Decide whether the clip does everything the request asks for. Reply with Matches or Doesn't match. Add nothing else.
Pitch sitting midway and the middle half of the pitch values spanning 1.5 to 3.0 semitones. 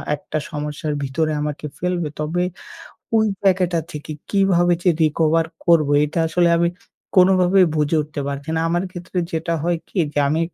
Matches